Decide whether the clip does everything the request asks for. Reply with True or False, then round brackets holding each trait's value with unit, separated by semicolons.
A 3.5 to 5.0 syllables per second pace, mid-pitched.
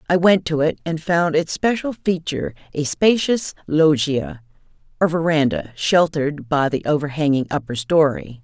True (4.7 syllables/s; 155 Hz)